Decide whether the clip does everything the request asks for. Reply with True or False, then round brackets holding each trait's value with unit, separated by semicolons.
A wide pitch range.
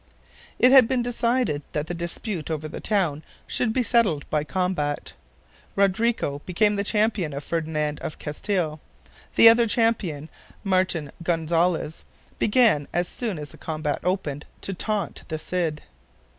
True (5.9 semitones)